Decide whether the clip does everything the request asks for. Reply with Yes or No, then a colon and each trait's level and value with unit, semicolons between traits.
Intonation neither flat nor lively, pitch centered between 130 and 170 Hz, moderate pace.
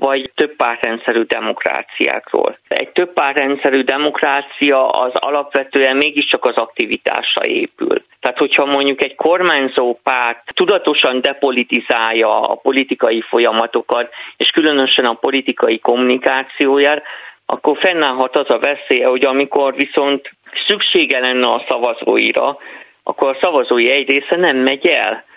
No: narrow, 1.8 semitones; low, 135 Hz; average, 120 wpm